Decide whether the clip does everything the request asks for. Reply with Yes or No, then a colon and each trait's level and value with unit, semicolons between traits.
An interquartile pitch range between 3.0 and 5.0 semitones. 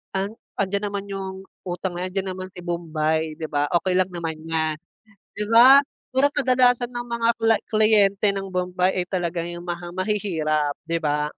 Yes: average, 3.8 semitones